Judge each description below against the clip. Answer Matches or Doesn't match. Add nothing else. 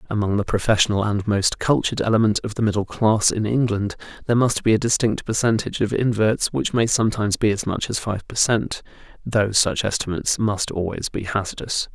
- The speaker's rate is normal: Matches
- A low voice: Matches